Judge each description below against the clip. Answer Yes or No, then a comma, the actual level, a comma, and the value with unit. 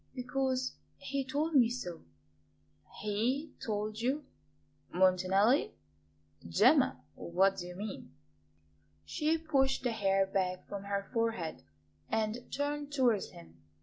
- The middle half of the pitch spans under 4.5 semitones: No, wide, 5.6 semitones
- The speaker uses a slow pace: Yes, slow, 115 wpm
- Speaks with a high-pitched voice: Yes, high, 225 Hz